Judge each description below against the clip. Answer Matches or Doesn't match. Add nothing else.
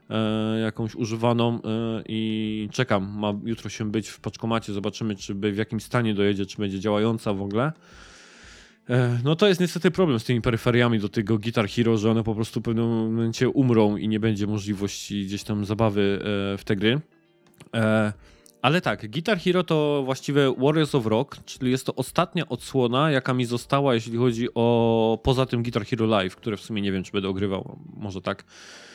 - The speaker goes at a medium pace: Doesn't match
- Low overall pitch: Matches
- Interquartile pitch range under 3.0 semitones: Doesn't match